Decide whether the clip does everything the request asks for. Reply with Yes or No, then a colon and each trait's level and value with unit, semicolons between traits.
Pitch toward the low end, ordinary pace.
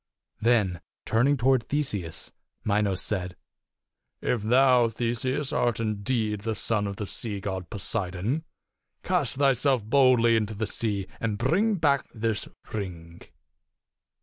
No: low, 115 Hz; slow, 125 wpm